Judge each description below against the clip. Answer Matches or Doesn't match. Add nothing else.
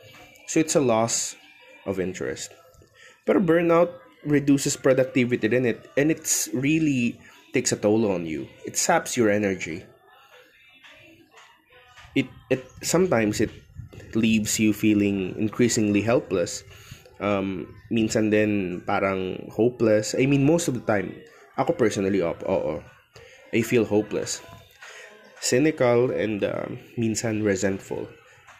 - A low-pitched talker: Matches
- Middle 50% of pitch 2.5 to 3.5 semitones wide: Doesn't match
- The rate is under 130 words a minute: Matches